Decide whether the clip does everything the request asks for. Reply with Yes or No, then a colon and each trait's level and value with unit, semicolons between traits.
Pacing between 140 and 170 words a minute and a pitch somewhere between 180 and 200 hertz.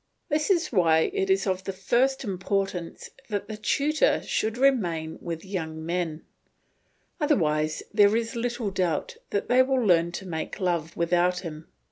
Yes: average, 150 wpm; high, 190 Hz